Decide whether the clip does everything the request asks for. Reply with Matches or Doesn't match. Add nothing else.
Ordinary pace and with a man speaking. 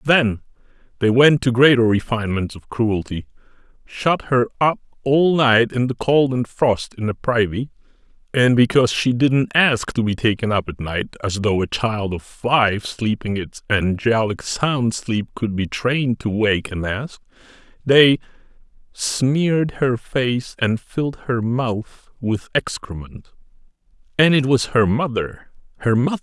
Matches